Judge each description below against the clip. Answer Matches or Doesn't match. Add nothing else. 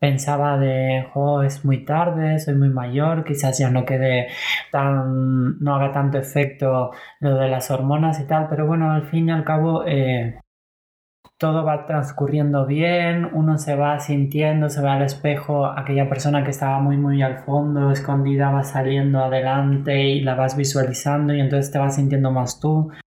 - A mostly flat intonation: Matches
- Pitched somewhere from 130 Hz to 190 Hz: Matches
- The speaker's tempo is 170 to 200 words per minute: Matches